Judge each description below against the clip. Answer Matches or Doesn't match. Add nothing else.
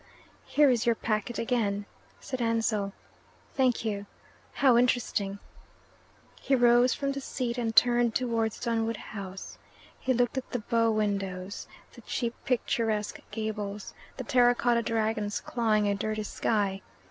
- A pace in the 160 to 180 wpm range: Doesn't match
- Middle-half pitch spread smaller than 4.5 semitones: Matches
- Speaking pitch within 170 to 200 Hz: Doesn't match